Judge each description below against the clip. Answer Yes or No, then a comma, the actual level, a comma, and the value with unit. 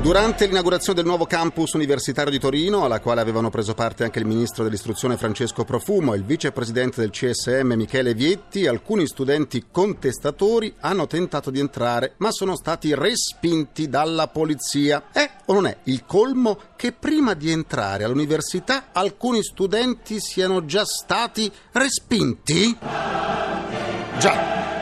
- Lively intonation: Yes, wide, 7.7 semitones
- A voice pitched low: No, medium, 155 Hz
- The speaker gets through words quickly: No, average, 140 wpm